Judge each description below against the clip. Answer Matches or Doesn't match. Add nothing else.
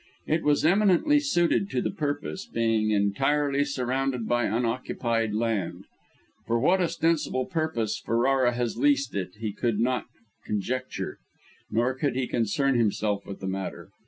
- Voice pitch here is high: Doesn't match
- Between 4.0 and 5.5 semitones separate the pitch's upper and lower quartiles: Matches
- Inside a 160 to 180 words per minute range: Doesn't match